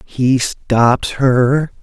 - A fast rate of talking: No, slow, 100 wpm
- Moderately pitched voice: No, low, 130 Hz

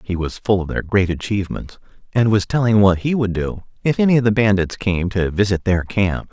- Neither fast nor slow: No, fast, 230 wpm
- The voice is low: Yes, low, 100 Hz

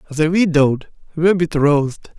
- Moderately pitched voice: Yes, medium, 155 Hz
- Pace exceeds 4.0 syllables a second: Yes, 5.2 syllables/s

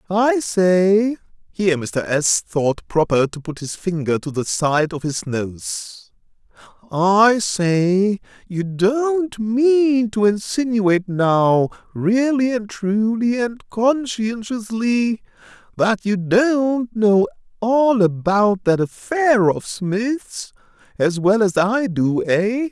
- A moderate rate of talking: No, slow, 115 wpm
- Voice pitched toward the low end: No, high, 205 Hz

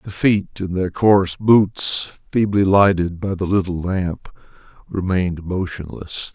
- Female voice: No, male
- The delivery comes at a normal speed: No, slow, 130 wpm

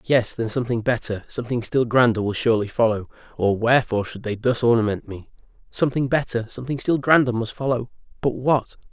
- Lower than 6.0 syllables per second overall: No, 6.1 syllables/s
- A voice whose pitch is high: No, low, 120 Hz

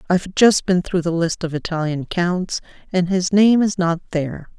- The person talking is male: No, female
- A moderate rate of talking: Yes, average, 195 wpm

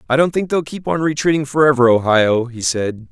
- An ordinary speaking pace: No, fast, 210 wpm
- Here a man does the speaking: Yes, male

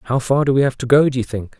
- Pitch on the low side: Yes, low, 130 Hz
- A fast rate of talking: Yes, fast, 375 wpm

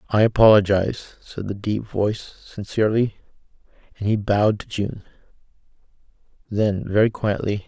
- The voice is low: Yes, low, 105 Hz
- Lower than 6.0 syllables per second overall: Yes, 5.1 syllables/s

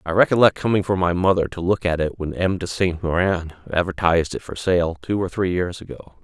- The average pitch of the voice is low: Yes, very low, 90 Hz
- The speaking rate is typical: No, fast, 230 wpm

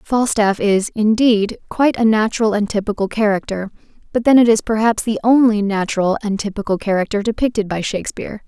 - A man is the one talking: No, female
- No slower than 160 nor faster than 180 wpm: Yes, average, 165 wpm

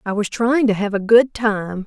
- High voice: Yes, high, 215 Hz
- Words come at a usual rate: No, fast, 260 wpm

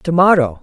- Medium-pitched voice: Yes, medium, 160 Hz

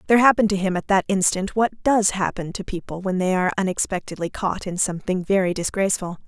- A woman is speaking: Yes, female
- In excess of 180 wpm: Yes, average, 200 wpm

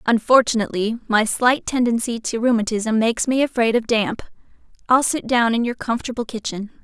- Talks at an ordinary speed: Yes, average, 160 wpm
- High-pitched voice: Yes, high, 230 Hz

